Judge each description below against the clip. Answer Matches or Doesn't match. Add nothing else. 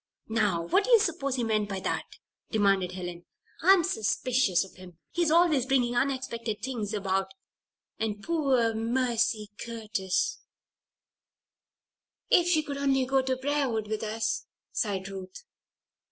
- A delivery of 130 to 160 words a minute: Matches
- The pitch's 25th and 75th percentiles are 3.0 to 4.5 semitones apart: Doesn't match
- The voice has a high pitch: Matches